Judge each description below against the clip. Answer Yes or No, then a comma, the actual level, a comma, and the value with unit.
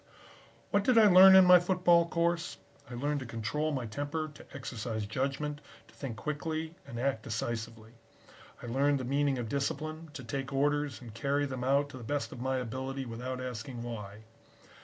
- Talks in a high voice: No, low, 135 Hz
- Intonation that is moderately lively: Yes, average, 3.9 semitones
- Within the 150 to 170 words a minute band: No, average, 180 wpm